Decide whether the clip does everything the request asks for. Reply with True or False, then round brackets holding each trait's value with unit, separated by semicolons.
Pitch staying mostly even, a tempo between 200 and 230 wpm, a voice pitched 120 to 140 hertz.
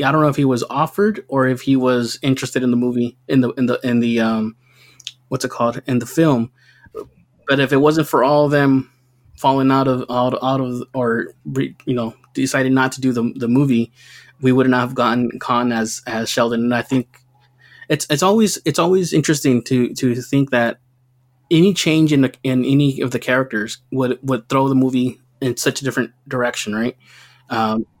True (1.9 semitones; 205 wpm; 130 Hz)